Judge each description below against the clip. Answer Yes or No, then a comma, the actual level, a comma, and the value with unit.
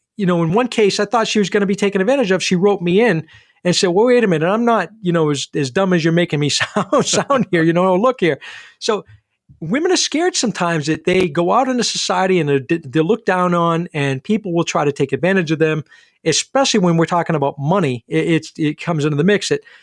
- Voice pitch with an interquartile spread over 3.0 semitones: Yes, average, 4.6 semitones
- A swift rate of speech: Yes, fast, 245 wpm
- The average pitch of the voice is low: No, medium, 180 Hz